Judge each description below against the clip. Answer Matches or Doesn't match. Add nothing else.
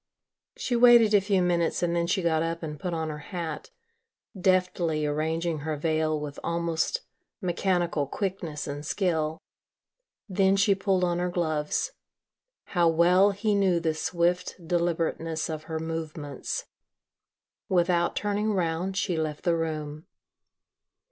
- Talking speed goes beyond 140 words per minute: Doesn't match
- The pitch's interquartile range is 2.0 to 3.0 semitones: Matches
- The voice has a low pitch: Doesn't match